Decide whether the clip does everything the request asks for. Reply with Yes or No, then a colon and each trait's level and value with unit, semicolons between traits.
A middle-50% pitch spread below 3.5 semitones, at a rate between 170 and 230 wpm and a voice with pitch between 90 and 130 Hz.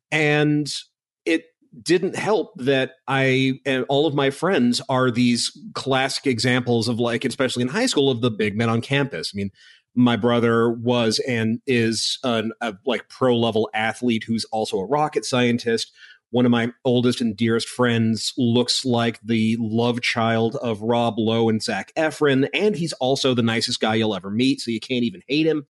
Yes: average, 2.9 semitones; average, 180 wpm; low, 120 Hz